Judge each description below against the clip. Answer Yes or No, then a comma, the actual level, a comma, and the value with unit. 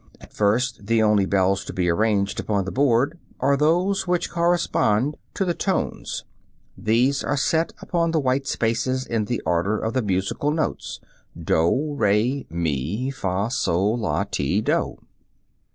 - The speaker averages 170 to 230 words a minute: No, average, 160 wpm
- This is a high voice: No, low, 115 Hz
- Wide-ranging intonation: Yes, wide, 6.1 semitones